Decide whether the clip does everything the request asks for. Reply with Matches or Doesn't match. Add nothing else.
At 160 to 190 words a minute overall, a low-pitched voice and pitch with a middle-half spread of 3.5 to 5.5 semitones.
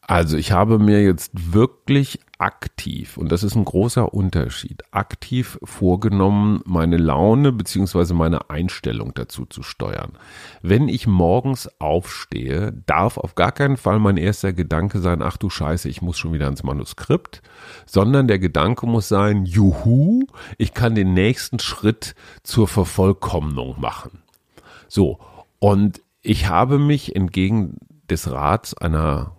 Doesn't match